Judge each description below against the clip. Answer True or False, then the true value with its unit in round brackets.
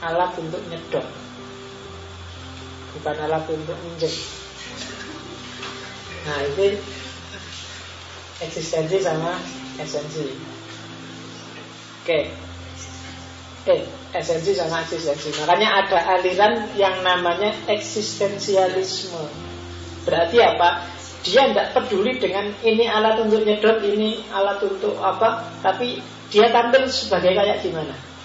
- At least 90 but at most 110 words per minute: True (95 wpm)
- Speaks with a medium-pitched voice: True (170 Hz)